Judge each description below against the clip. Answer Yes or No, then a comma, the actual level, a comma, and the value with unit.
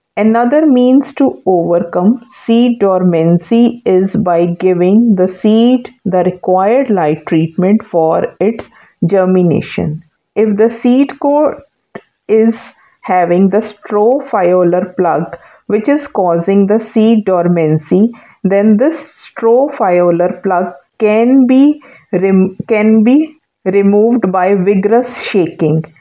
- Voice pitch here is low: No, high, 205 Hz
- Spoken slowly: Yes, slow, 105 wpm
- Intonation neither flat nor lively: Yes, average, 4.6 semitones